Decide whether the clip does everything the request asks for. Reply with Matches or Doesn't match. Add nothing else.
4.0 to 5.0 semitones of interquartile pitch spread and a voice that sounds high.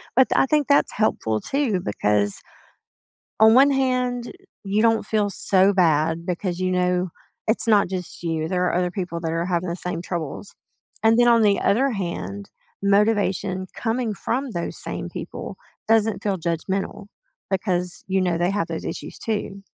Matches